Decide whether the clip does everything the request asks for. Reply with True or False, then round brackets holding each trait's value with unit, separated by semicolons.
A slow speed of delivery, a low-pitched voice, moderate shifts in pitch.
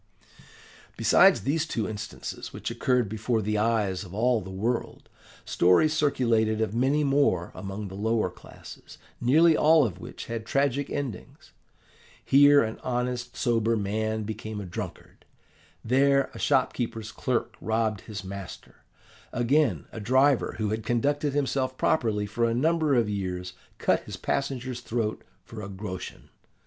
False (145 wpm; 115 Hz; 4.2 semitones)